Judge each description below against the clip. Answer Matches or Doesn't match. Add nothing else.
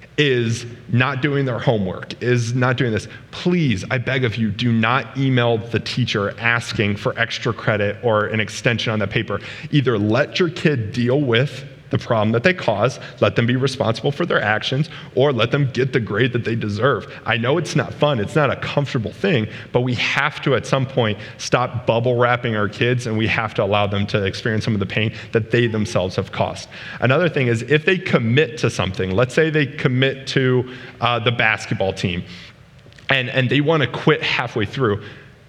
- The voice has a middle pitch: Doesn't match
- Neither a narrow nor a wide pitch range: Matches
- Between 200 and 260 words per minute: Matches